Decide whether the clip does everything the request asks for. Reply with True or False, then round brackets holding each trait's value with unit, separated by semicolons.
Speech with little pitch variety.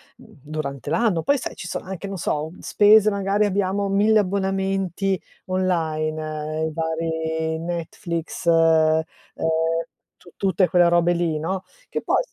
False (3.3 semitones)